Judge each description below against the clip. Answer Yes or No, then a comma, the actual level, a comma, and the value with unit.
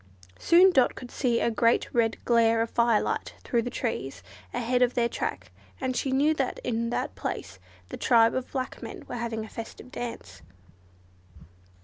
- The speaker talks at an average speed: Yes, average, 170 wpm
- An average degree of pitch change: No, narrow, 1.8 semitones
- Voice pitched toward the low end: No, high, 235 Hz